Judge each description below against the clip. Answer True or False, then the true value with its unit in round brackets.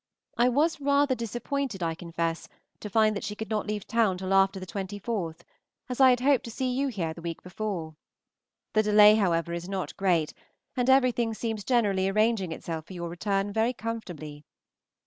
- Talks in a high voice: True (210 Hz)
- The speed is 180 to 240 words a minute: True (185 wpm)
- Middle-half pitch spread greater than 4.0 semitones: True (4.7 semitones)